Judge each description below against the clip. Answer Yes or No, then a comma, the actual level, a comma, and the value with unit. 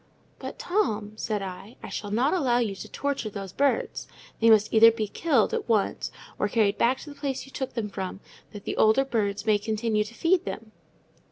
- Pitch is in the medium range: No, high, 220 Hz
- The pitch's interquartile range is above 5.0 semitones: No, average, 4.0 semitones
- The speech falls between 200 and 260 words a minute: Yes, fast, 205 wpm